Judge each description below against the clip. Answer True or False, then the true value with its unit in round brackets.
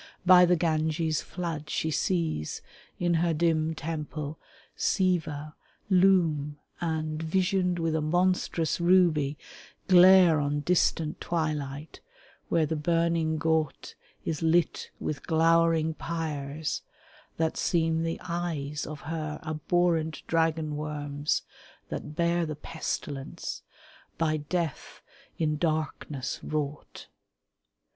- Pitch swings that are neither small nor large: False (1.9 semitones)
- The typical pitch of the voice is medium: True (160 Hz)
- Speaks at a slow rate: True (105 wpm)